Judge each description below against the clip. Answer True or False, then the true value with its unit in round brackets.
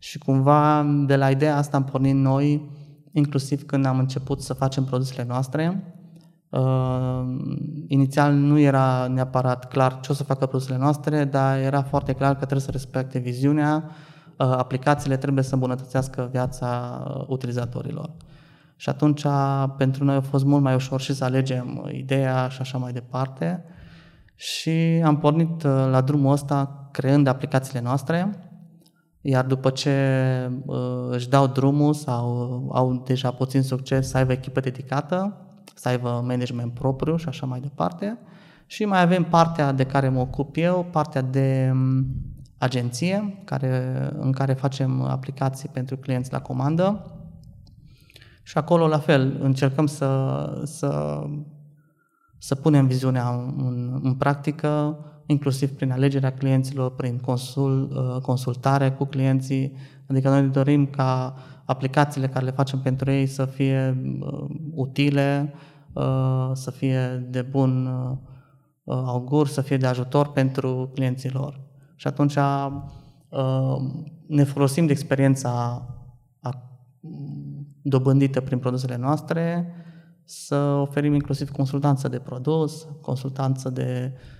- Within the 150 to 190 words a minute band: False (125 wpm)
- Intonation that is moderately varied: False (2.1 semitones)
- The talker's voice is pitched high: False (135 Hz)